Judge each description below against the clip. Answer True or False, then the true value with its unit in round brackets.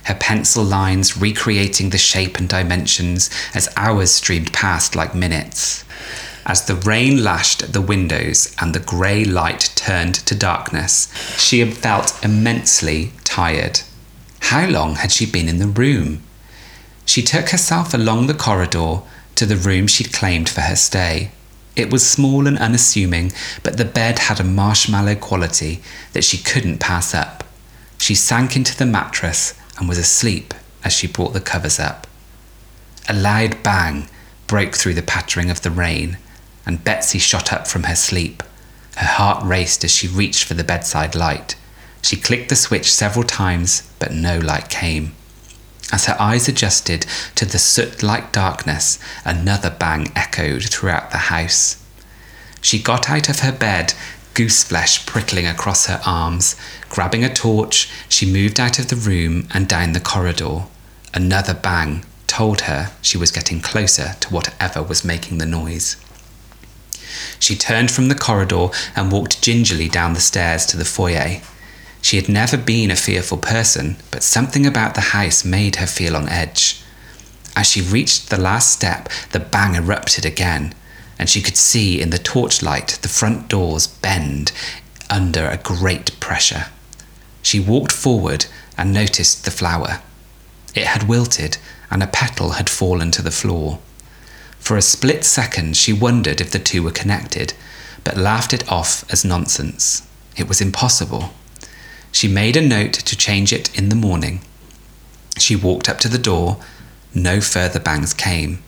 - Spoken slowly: False (160 wpm)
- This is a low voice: True (95 Hz)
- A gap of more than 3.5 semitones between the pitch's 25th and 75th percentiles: True (4.3 semitones)